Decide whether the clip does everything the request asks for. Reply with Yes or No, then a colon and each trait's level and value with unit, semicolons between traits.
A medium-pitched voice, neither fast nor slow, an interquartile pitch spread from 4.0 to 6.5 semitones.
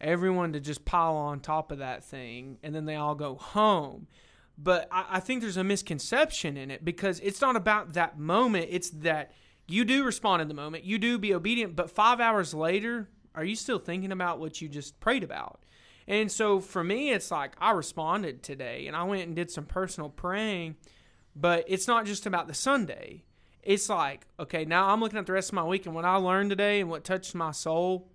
No: medium, 180 Hz; fast, 215 wpm; average, 4.4 semitones